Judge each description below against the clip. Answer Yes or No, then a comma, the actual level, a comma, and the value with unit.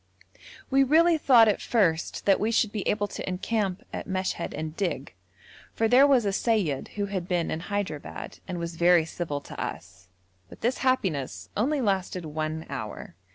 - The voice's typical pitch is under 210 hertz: Yes, high, 190 Hz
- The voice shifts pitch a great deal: Yes, wide, 5.8 semitones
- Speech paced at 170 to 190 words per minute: Yes, average, 175 wpm